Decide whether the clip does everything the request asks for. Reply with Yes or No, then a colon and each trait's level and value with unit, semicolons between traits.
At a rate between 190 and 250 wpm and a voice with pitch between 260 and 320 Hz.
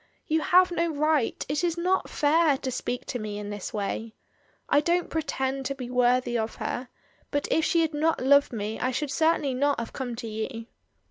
Yes: fast, 205 wpm; very high, 275 Hz